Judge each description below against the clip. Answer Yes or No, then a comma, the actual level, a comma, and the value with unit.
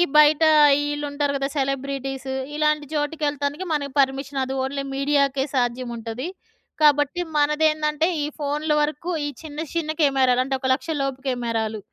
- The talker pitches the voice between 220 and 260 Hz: No, very high, 280 Hz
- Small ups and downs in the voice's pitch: Yes, narrow, 2.0 semitones